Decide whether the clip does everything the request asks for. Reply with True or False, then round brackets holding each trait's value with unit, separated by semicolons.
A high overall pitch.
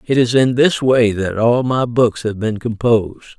False (115 Hz)